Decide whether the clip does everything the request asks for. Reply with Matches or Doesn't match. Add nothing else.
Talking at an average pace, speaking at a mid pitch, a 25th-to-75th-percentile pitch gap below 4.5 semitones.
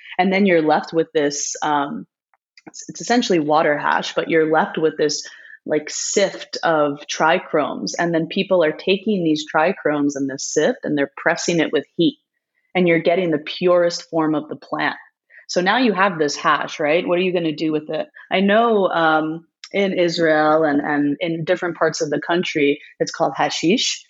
Doesn't match